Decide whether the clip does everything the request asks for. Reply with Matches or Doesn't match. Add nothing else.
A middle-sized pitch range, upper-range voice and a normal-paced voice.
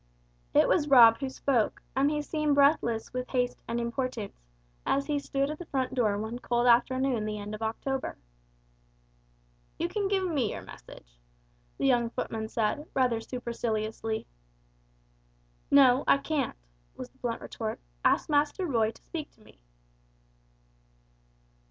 Matches